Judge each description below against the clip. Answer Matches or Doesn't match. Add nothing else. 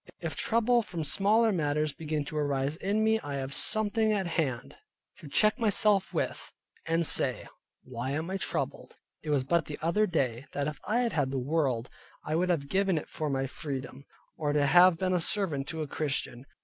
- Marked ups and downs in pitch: Matches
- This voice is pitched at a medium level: Matches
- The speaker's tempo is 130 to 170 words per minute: Doesn't match